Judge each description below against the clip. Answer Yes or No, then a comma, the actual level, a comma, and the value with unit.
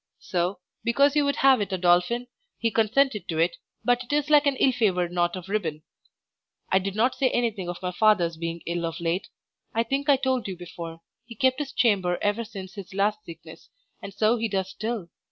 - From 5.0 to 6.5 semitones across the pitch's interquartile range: Yes, wide, 5.6 semitones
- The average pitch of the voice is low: No, high, 205 Hz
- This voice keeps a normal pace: No, fast, 210 wpm